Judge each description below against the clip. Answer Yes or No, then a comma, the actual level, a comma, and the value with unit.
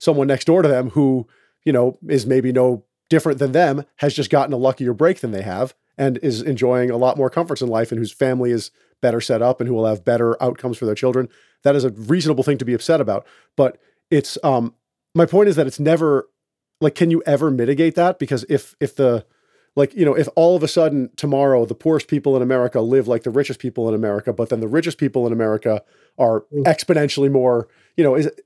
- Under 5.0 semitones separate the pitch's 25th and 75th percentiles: Yes, average, 3.5 semitones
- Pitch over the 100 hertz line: Yes, low, 135 Hz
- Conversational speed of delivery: No, fast, 230 wpm